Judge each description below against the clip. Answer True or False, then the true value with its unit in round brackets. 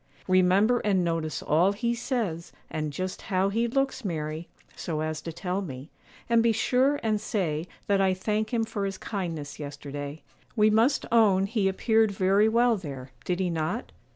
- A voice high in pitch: True (195 Hz)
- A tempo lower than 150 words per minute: False (175 wpm)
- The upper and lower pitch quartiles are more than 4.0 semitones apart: True (5.4 semitones)